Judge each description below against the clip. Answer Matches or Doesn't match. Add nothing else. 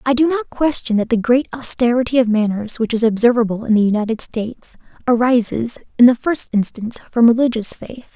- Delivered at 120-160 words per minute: Doesn't match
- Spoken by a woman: Matches